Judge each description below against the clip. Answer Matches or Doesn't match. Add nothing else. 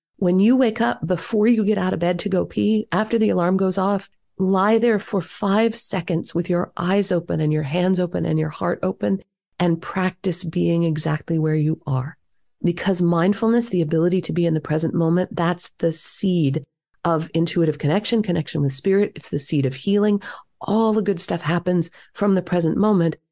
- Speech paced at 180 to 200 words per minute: Matches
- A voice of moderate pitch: Matches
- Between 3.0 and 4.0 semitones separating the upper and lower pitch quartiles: Matches